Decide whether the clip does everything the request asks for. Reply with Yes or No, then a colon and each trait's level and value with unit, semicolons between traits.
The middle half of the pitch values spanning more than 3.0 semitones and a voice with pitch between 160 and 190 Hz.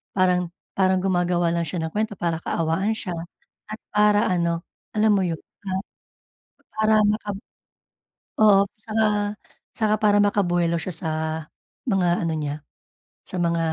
Yes: average, 3.6 semitones; medium, 185 Hz